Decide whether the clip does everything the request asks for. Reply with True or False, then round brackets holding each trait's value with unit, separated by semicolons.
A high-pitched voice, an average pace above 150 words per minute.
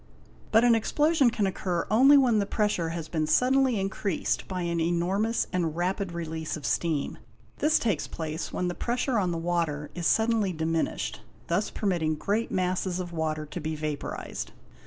False (180 Hz; 170 wpm)